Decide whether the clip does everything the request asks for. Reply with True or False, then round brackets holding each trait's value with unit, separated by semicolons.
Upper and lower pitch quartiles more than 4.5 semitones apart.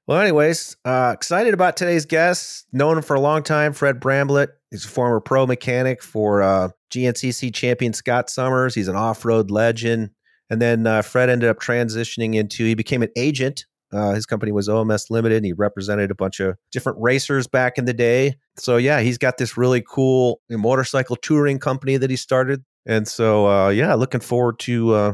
False (3.0 semitones)